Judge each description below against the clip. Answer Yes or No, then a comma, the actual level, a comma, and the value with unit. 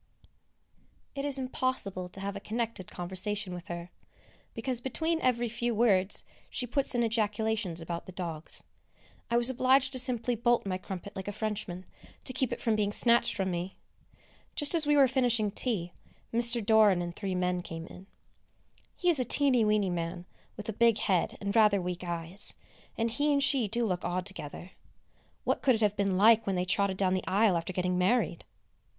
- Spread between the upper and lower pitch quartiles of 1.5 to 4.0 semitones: No, average, 4.6 semitones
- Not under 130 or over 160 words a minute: No, average, 190 wpm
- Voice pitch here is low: No, high, 210 Hz